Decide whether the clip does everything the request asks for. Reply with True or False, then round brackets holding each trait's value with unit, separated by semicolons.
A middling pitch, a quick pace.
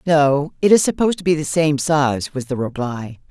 True (150 Hz; 220 wpm)